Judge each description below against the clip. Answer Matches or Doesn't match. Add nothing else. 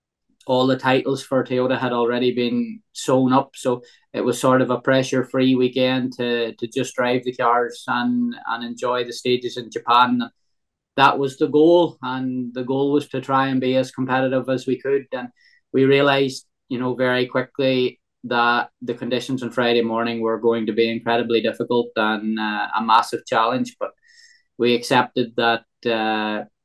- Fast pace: Doesn't match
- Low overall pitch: Matches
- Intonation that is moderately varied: Doesn't match